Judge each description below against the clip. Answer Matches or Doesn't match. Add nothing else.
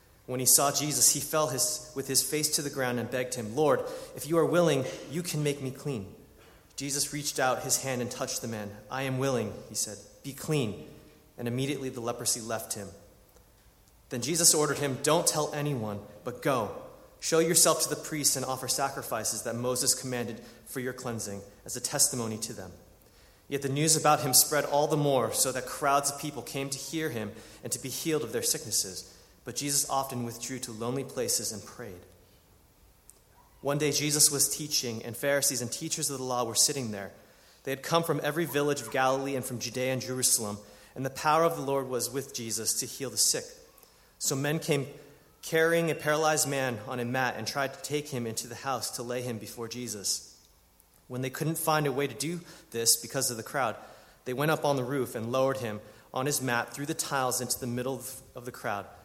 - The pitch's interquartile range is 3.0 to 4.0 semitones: Matches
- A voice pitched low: Matches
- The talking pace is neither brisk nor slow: Doesn't match